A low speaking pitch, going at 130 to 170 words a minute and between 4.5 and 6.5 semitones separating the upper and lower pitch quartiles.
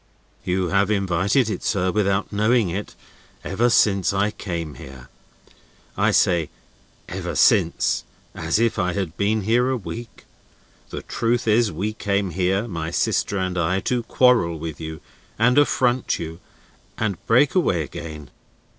Yes: low, 100 Hz; average, 145 wpm; average, 4.8 semitones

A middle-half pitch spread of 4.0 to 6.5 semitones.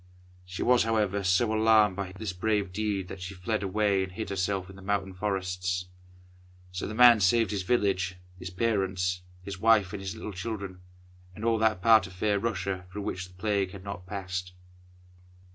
No: average, 2.8 semitones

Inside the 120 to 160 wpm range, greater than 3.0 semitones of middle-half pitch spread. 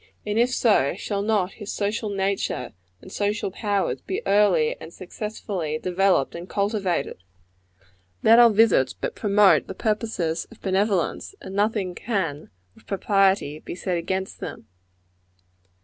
No: slow, 135 wpm; average, 2.7 semitones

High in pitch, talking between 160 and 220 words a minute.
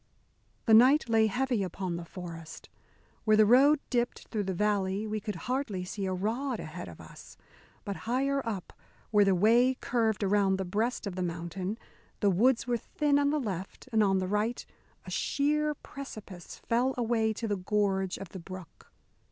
Yes: high, 210 Hz; average, 180 wpm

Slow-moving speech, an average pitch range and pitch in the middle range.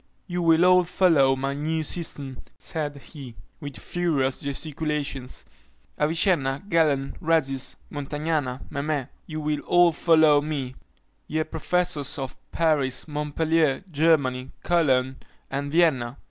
Yes: slow, 115 wpm; average, 3.1 semitones; medium, 150 Hz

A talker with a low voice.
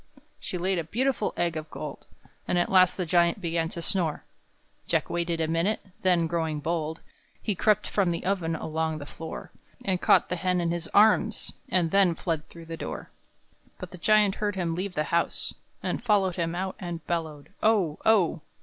No: medium, 175 Hz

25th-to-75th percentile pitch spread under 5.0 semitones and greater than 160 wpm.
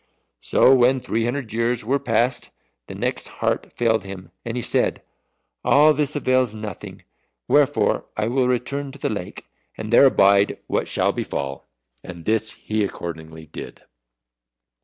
No: average, 4.2 semitones; average, 150 wpm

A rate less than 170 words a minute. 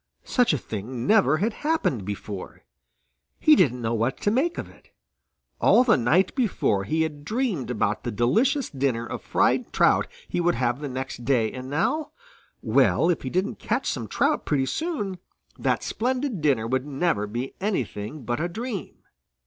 No: average, 175 wpm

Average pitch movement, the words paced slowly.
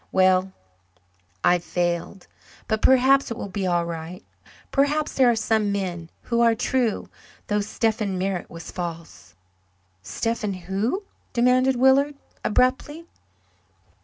No: wide, 6.0 semitones; slow, 120 wpm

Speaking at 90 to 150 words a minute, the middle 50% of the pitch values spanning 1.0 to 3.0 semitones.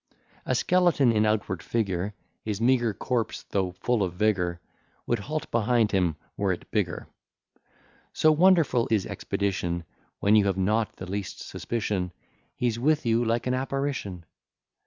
No: average, 145 wpm; average, 4.3 semitones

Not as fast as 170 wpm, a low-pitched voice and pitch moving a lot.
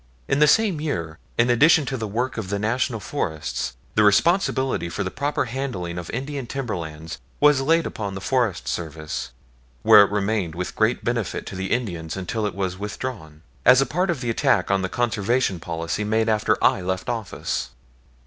No: average, 185 wpm; low, 105 Hz; wide, 6.2 semitones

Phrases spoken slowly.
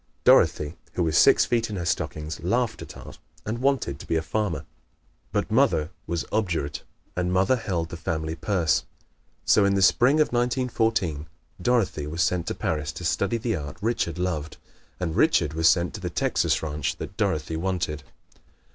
No: average, 175 wpm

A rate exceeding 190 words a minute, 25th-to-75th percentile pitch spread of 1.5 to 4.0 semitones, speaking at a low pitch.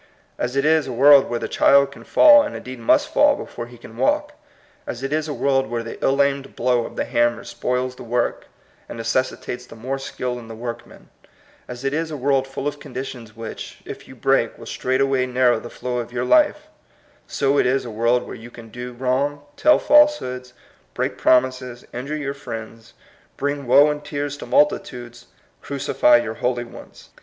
Yes: average, 200 wpm; narrow, 2.6 semitones; low, 130 Hz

